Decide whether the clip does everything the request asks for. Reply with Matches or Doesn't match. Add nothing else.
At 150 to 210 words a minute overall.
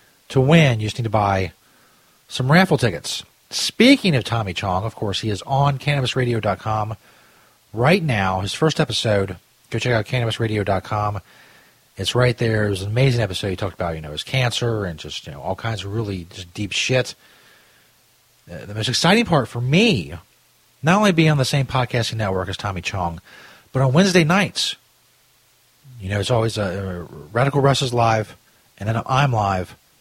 Matches